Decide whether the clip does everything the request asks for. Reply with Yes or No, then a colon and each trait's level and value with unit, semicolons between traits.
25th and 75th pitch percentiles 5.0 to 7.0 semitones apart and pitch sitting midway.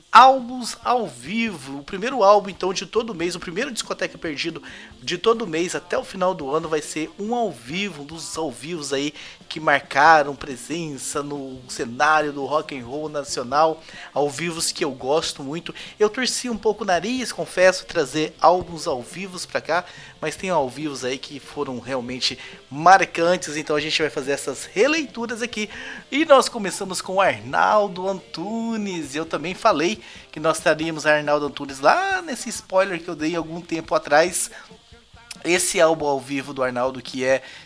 Yes: average, 5.3 semitones; medium, 165 Hz